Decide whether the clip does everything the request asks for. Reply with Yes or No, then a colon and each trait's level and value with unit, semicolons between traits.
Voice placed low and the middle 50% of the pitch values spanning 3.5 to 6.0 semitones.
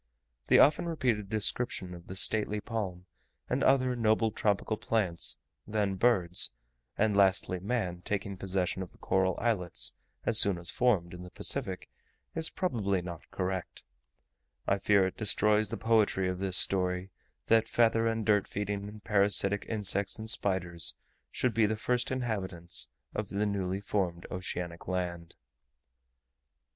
No: low, 100 Hz; average, 3.1 semitones